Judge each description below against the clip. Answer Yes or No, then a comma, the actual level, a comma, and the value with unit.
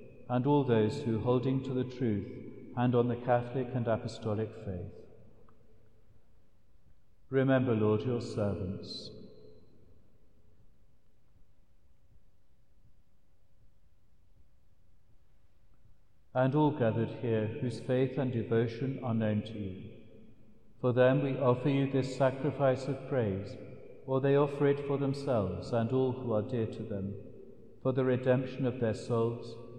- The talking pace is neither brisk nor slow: No, slow, 120 wpm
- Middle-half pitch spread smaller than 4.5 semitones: Yes, average, 3.2 semitones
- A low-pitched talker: Yes, low, 115 Hz